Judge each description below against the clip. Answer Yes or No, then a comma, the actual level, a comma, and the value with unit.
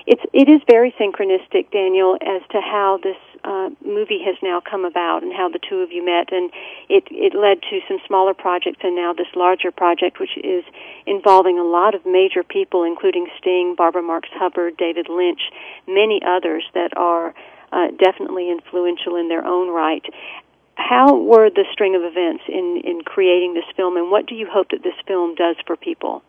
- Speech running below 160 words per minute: No, average, 190 wpm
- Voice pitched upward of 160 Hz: Yes, high, 190 Hz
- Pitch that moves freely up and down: Yes, wide, 7.9 semitones